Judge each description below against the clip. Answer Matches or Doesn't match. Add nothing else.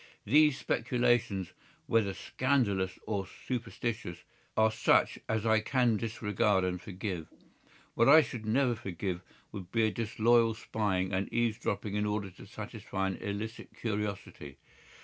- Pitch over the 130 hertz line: Doesn't match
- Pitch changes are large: Doesn't match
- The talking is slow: Matches